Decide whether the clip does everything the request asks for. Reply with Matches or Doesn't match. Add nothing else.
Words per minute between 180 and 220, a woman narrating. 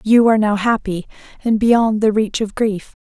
Matches